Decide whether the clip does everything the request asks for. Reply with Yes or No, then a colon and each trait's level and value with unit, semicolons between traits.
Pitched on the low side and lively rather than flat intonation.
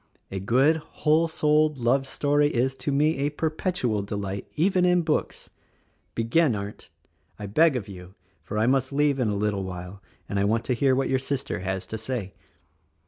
Yes: low, 130 Hz; wide, 6.6 semitones